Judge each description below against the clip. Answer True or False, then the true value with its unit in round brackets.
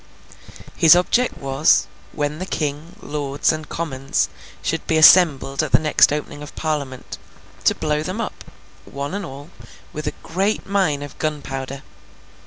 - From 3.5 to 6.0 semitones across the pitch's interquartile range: False (2.7 semitones)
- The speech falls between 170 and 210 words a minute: False (150 wpm)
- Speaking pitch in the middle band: True (150 Hz)